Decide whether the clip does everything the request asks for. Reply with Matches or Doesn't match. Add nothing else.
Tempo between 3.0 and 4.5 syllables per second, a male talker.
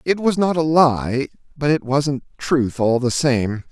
Matches